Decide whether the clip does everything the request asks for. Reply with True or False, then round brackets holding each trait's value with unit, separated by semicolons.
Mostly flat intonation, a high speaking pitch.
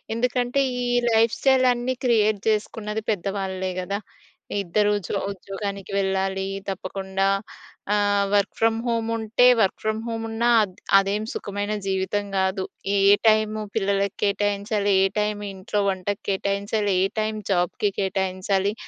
True (2.0 semitones; 205 Hz)